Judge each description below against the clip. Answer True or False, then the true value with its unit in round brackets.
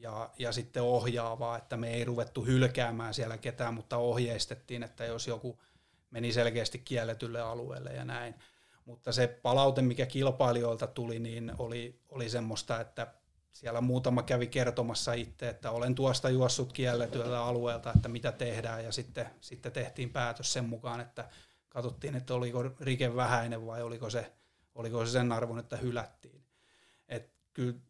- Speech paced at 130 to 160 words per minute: True (155 wpm)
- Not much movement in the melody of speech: True (1.2 semitones)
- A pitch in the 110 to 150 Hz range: True (120 Hz)